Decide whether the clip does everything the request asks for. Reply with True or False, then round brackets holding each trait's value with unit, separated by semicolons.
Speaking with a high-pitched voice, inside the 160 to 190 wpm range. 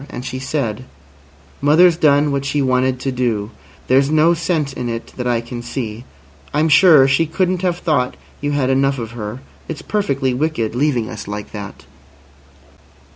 False (135 Hz; 170 wpm)